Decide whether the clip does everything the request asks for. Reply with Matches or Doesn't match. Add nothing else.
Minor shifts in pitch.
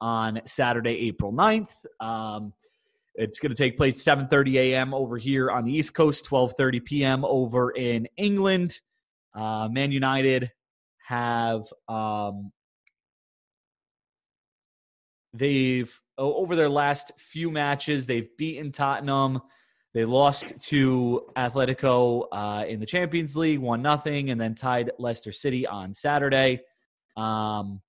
Doesn't match